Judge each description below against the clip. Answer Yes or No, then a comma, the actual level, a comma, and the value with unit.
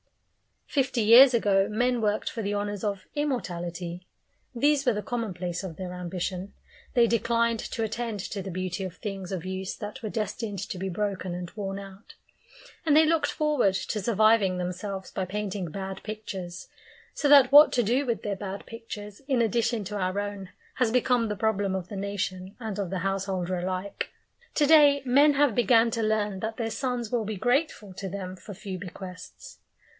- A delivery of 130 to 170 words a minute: No, average, 185 wpm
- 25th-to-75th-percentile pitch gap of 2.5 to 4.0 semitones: Yes, average, 3.7 semitones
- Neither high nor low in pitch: No, high, 205 Hz